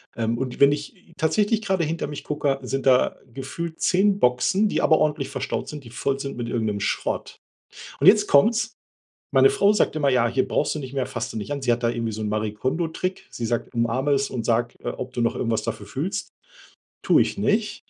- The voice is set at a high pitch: No, low, 135 Hz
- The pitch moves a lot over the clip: Yes, wide, 6.0 semitones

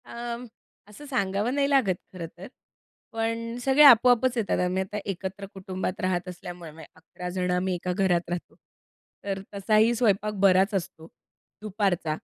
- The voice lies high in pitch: Yes, high, 195 Hz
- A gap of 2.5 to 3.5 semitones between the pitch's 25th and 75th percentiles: No, average, 4.0 semitones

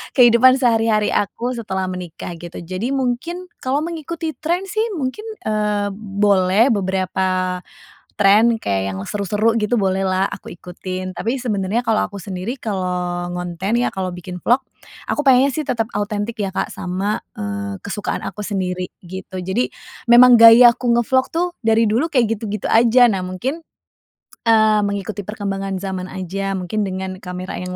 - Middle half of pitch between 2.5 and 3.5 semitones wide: No, average, 4.3 semitones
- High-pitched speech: Yes, high, 205 Hz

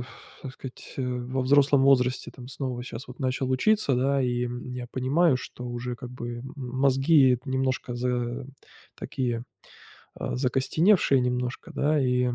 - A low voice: Yes, low, 130 Hz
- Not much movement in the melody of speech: Yes, narrow, 1.6 semitones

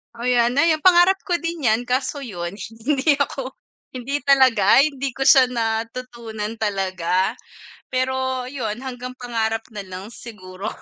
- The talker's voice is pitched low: No, high, 245 Hz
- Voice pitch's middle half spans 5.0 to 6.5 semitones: No, average, 3.7 semitones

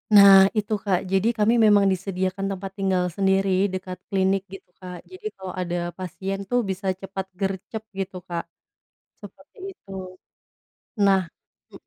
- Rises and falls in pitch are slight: Yes, narrow, 1.0 semitones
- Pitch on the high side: Yes, high, 195 Hz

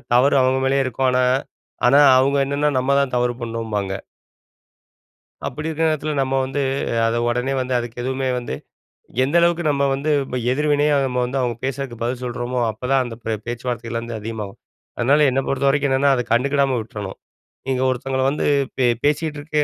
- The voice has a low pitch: Yes, low, 130 Hz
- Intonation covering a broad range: No, narrow, 2.6 semitones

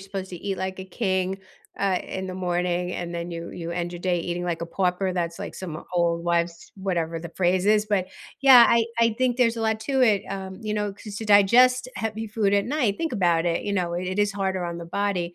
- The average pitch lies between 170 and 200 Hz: Yes, high, 190 Hz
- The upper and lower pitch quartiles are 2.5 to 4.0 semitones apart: Yes, average, 3.2 semitones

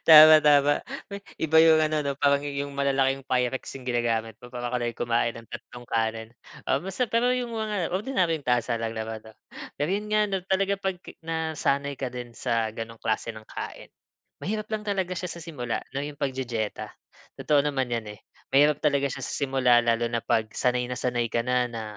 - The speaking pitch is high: No, low, 135 Hz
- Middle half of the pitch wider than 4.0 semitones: Yes, average, 5.2 semitones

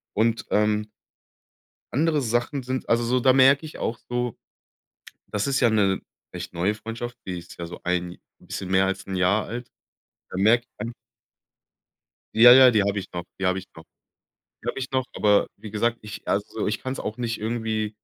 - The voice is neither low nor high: No, low, 110 Hz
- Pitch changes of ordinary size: Yes, average, 3.8 semitones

